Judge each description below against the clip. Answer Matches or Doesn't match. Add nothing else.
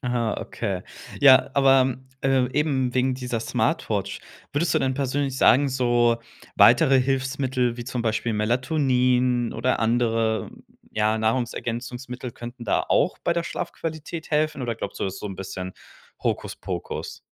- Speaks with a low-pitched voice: Matches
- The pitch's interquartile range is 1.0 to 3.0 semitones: Matches